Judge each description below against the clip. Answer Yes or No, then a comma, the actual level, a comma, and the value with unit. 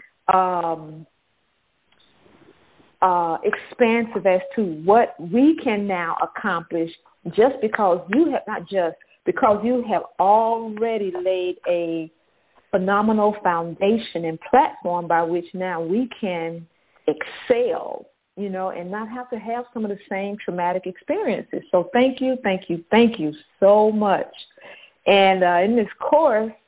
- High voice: Yes, high, 195 Hz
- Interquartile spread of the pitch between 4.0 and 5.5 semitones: Yes, average, 4.5 semitones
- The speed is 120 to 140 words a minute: Yes, slow, 135 wpm